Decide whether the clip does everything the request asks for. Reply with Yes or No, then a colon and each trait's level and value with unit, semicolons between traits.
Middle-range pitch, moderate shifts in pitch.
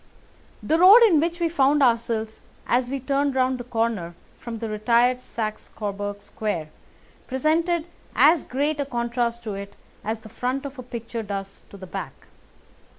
No: high, 240 Hz; average, 4.4 semitones